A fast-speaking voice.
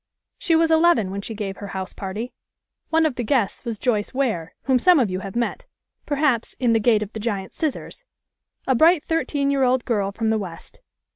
Yes: fast, 210 wpm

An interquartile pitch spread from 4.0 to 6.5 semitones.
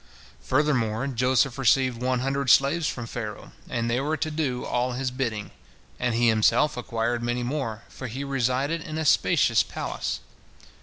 No: average, 2.7 semitones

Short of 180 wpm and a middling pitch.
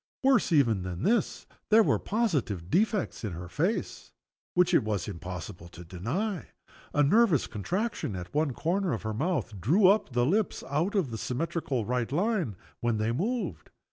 Yes: average, 170 wpm; medium, 145 Hz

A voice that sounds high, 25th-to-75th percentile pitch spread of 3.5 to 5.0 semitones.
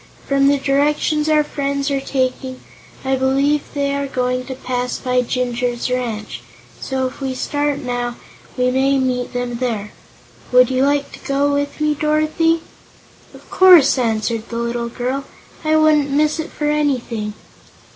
No: very high, 270 Hz; narrow, 2.4 semitones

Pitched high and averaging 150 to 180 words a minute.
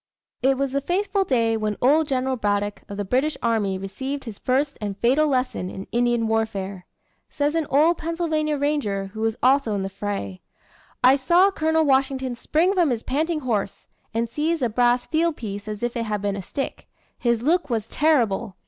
No: very high, 250 Hz; average, 190 wpm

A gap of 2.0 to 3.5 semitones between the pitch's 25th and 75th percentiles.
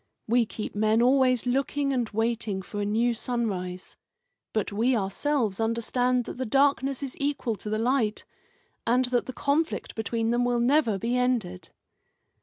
Yes: average, 2.9 semitones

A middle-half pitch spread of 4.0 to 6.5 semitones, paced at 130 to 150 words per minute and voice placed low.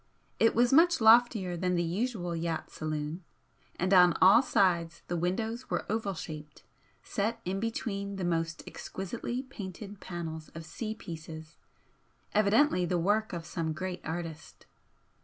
No: average, 4.7 semitones; average, 140 wpm; medium, 185 Hz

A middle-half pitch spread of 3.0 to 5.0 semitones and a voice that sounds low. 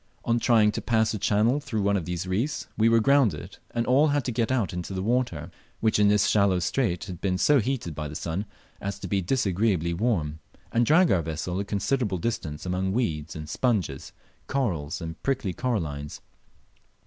No: wide, 5.5 semitones; low, 100 Hz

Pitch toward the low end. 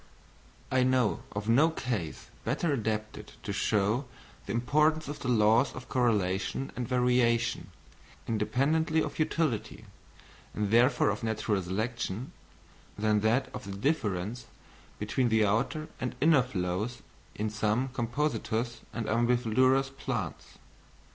Yes: low, 120 Hz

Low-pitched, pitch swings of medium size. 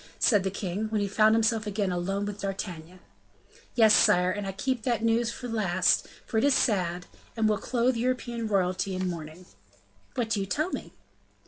No: high, 205 Hz; average, 3.5 semitones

